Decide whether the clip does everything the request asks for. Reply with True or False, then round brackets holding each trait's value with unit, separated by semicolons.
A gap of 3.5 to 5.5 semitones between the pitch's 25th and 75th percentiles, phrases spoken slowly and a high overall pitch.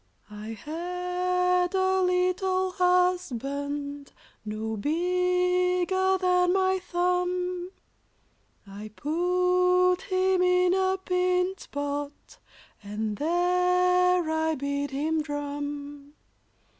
True (3.9 semitones; 85 wpm; 360 Hz)